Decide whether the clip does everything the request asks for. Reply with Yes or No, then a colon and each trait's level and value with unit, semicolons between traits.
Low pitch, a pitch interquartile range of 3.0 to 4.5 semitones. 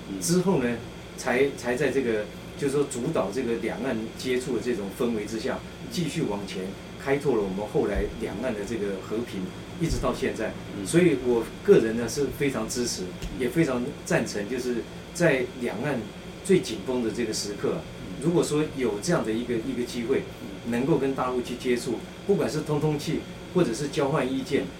No: low, 125 Hz; average, 4.9 semitones